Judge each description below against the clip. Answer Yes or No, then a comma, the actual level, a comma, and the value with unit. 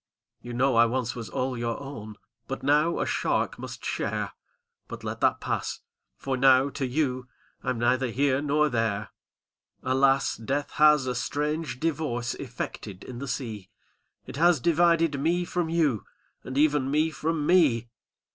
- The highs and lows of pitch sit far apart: No, average, 3.8 semitones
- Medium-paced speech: Yes, average, 160 wpm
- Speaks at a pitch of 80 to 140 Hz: Yes, low, 135 Hz